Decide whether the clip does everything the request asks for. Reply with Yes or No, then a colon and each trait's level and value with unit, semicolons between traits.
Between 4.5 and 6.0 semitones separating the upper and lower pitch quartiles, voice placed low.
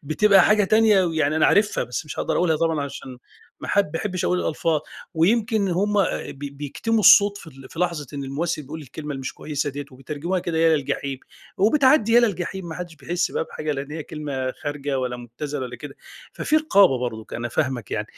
No: average, 5.3 semitones; medium, 155 Hz